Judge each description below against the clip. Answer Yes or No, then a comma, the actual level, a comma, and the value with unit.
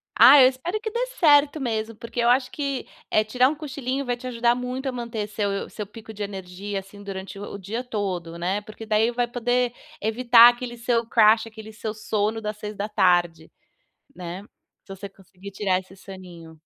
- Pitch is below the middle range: No, high, 220 Hz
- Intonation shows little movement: No, average, 3.7 semitones